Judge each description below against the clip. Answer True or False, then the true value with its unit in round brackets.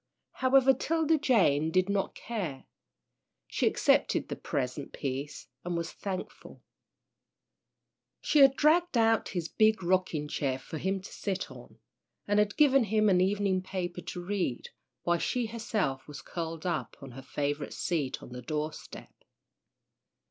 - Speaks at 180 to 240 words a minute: False (150 wpm)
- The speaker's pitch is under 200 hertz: True (185 Hz)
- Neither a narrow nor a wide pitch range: False (6.4 semitones)